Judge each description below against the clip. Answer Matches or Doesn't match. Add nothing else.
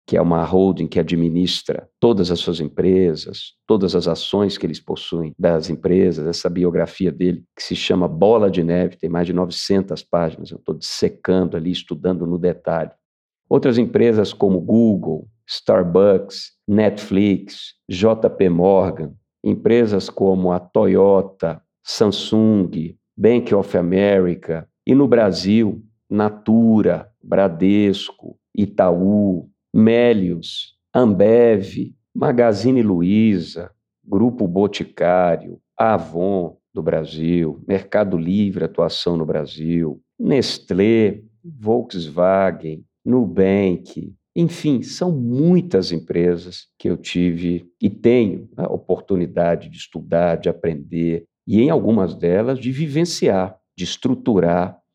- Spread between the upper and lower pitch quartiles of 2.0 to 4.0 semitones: Matches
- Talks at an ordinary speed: Doesn't match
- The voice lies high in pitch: Doesn't match